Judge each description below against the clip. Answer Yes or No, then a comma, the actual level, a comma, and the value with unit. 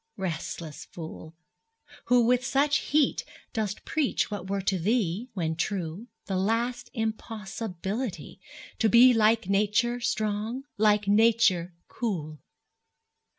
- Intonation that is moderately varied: Yes, average, 3.9 semitones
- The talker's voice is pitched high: Yes, high, 210 Hz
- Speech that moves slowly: Yes, slow, 110 wpm